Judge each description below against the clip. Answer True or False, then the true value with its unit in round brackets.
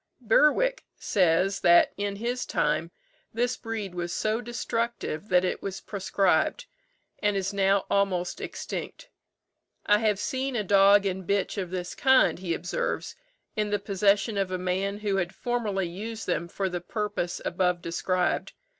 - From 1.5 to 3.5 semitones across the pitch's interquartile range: True (2.9 semitones)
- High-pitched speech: True (200 Hz)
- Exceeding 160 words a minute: False (155 wpm)